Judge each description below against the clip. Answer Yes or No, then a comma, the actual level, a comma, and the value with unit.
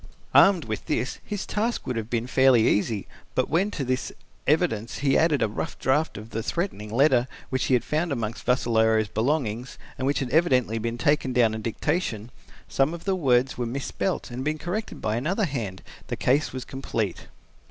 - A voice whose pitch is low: Yes, low, 130 Hz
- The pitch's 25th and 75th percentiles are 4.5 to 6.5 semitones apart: Yes, average, 5.0 semitones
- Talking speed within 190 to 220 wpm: Yes, average, 195 wpm